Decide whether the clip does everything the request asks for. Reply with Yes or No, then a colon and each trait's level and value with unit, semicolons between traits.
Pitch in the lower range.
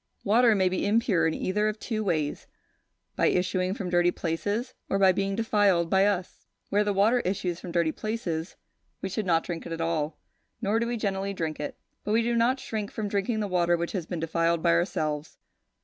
No: high, 190 Hz